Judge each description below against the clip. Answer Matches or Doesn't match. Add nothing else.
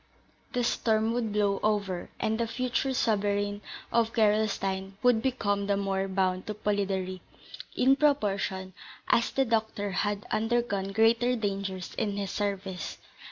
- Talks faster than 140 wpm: Doesn't match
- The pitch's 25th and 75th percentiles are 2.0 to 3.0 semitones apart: Matches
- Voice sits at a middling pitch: Doesn't match